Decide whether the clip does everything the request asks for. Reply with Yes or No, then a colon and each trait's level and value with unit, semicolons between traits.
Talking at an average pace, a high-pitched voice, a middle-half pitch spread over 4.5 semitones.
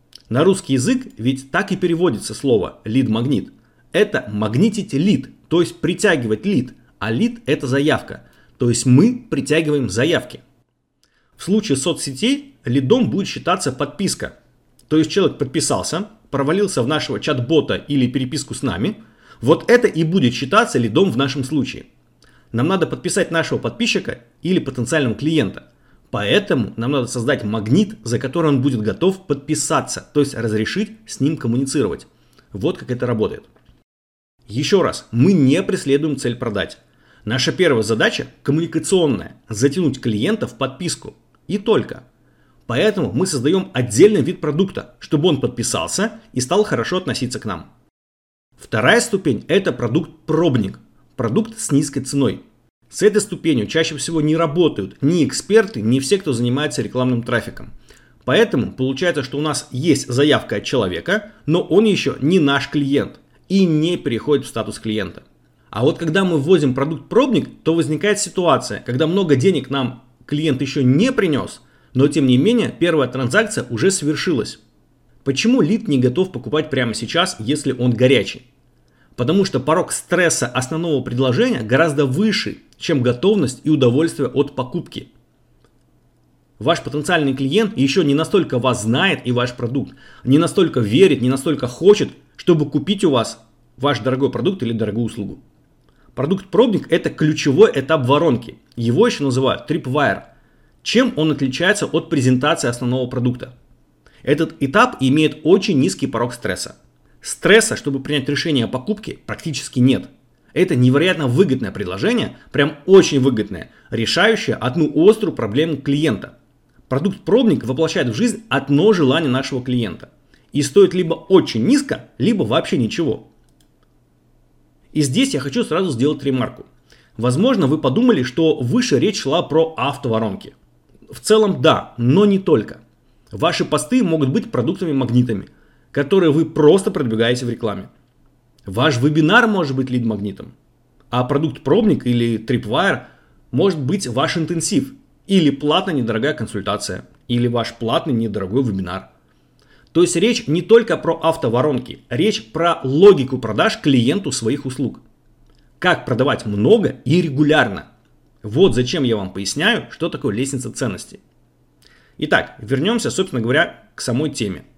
No: average, 140 wpm; medium, 140 Hz; average, 5.1 semitones